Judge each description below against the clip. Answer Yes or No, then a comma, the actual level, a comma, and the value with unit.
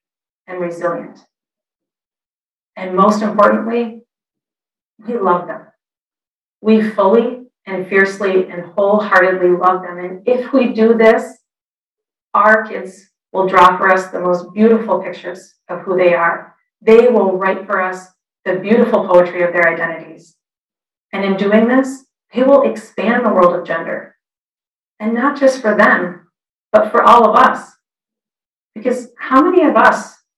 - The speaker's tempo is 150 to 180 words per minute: No, average, 140 wpm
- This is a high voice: Yes, high, 195 Hz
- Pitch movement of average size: Yes, average, 4.1 semitones